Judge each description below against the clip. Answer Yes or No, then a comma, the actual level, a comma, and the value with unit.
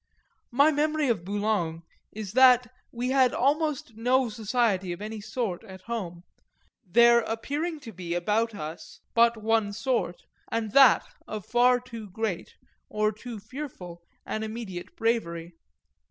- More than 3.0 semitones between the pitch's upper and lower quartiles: Yes, average, 3.7 semitones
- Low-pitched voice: No, high, 225 Hz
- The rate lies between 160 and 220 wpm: No, average, 140 wpm